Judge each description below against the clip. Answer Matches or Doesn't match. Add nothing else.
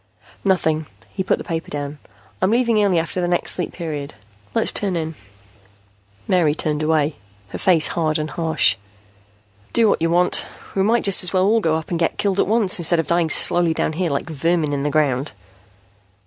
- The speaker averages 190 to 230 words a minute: Matches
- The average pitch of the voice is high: Doesn't match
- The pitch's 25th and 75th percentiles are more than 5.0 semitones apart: Doesn't match